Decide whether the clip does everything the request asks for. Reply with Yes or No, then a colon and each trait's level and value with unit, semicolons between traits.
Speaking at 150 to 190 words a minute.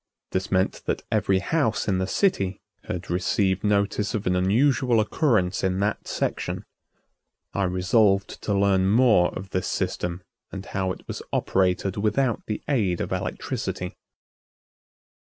No: average, 140 wpm